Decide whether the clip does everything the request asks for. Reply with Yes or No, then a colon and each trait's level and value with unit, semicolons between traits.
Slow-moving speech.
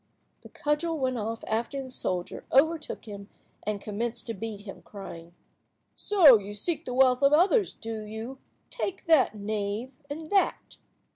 No: average, 155 wpm